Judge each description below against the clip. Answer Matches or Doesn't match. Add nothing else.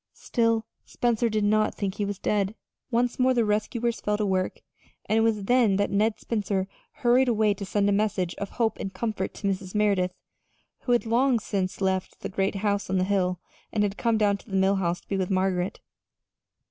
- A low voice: Doesn't match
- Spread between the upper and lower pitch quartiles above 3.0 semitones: Doesn't match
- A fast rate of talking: Matches